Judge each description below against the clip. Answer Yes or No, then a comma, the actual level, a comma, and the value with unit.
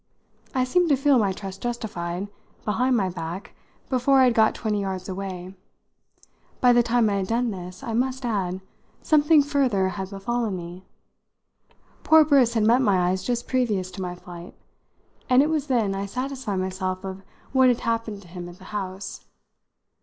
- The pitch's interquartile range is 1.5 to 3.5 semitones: No, average, 5.1 semitones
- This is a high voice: Yes, high, 210 Hz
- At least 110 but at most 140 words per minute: No, average, 175 wpm